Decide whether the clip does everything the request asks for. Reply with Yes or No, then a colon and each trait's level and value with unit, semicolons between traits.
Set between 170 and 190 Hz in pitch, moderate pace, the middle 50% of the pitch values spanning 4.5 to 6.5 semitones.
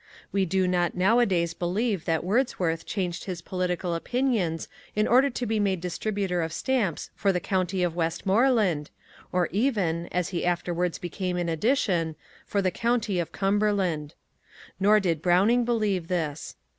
No: medium, 185 Hz; average, 150 wpm; average, 3.5 semitones